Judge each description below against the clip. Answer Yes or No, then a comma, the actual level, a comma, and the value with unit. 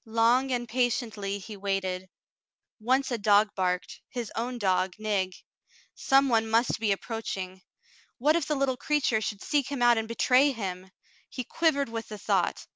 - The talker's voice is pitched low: No, high, 225 Hz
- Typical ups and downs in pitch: Yes, average, 4.2 semitones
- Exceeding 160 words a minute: Yes, average, 170 wpm